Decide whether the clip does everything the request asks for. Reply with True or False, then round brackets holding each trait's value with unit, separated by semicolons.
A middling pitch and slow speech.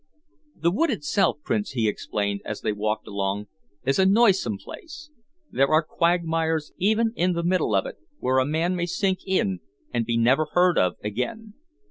False (165 Hz; 175 wpm)